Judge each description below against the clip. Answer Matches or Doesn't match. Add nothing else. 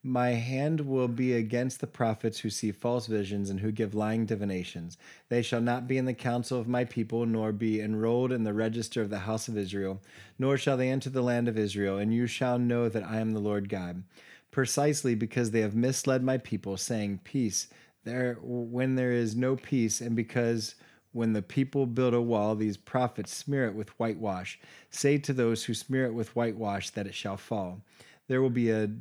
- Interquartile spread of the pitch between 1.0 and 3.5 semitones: Matches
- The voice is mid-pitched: Doesn't match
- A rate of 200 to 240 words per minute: Matches